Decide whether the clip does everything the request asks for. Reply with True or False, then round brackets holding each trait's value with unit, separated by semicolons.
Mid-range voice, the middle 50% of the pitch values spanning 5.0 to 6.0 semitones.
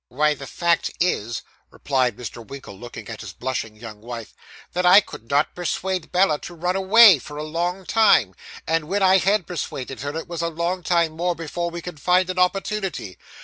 True (165 Hz; 5.6 semitones)